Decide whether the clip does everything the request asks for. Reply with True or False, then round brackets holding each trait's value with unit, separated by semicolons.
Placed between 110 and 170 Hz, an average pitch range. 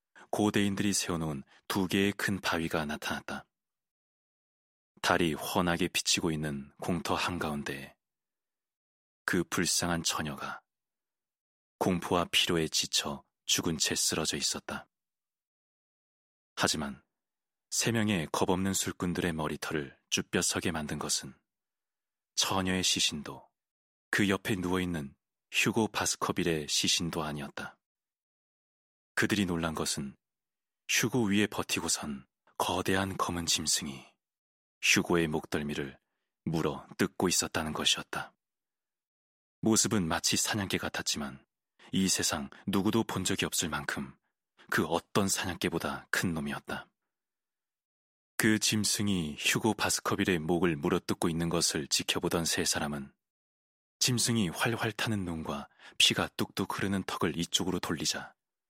False (90 Hz; 3.8 semitones)